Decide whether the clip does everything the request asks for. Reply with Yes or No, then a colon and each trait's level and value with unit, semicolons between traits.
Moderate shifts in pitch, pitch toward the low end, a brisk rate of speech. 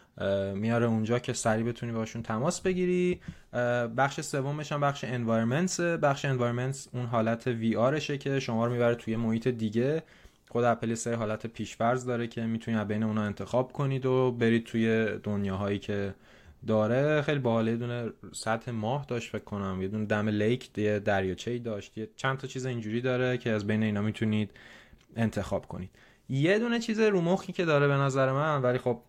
Yes: average, 3.4 semitones; low, 120 Hz; fast, 175 wpm